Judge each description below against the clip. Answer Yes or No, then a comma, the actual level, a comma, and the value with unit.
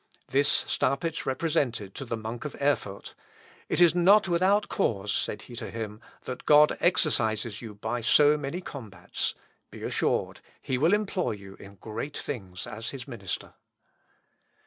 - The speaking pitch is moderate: No, low, 130 Hz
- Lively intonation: Yes, wide, 6.2 semitones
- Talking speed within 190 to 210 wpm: No, average, 150 wpm